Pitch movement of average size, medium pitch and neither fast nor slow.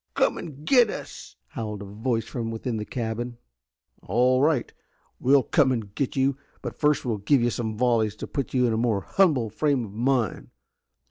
No: average, 3.3 semitones; low, 120 Hz; average, 190 wpm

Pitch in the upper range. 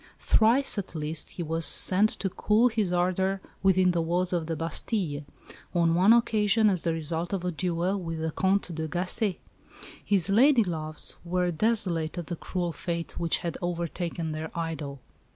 No: medium, 175 Hz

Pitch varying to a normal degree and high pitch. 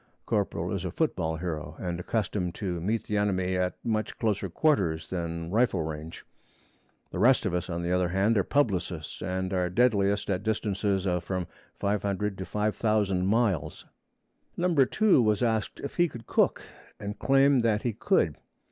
No: average, 3.5 semitones; low, 100 Hz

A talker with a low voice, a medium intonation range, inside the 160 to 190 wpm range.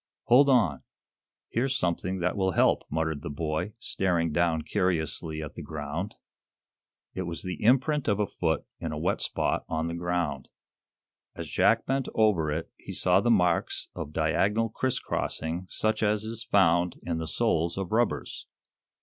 Yes: very low, 85 Hz; average, 4.8 semitones; average, 165 wpm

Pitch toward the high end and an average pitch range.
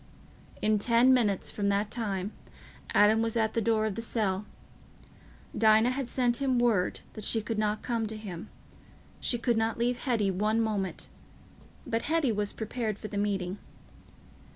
No: high, 220 Hz; narrow, 2.2 semitones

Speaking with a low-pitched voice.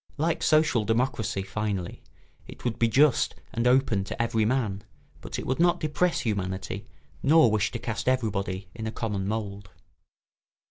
Yes: low, 115 Hz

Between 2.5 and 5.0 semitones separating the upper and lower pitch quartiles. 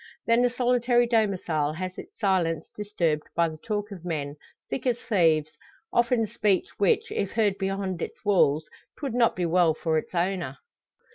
No: wide, 5.6 semitones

